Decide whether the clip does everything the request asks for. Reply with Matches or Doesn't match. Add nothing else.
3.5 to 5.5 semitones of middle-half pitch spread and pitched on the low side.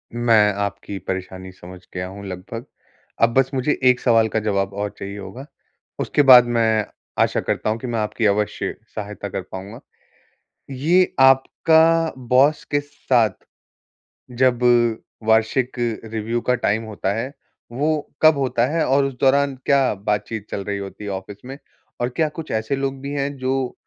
Matches